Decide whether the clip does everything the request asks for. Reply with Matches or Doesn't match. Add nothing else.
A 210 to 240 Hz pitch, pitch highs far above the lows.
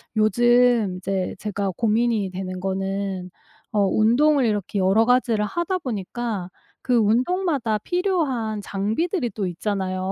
Doesn't match